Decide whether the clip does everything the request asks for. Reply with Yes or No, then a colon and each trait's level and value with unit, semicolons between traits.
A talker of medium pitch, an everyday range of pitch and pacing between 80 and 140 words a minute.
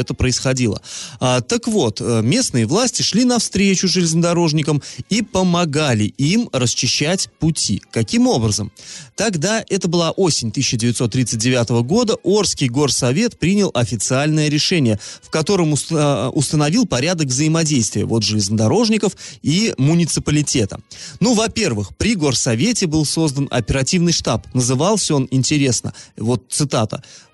No: medium, 150 Hz; wide, 6.5 semitones; slow, 110 wpm